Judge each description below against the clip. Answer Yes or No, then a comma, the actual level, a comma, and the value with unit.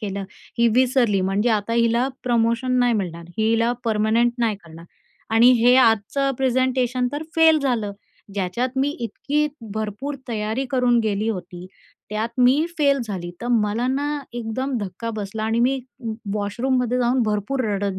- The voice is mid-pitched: No, high, 230 Hz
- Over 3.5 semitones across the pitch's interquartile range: No, average, 3.2 semitones